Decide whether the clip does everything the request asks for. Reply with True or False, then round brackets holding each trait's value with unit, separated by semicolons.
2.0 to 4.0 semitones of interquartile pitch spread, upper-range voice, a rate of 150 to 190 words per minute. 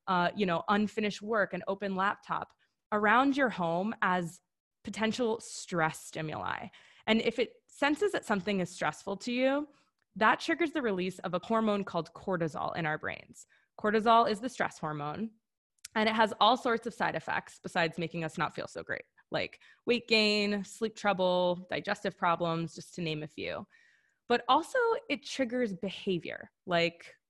False (4.5 semitones; 205 Hz; 165 wpm)